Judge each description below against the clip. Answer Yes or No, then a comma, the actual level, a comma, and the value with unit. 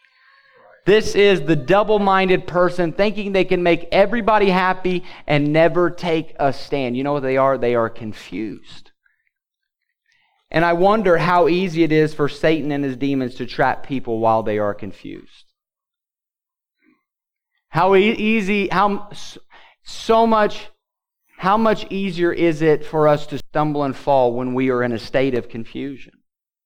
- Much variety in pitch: Yes, wide, 6.7 semitones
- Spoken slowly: No, average, 150 wpm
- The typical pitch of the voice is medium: Yes, medium, 170 Hz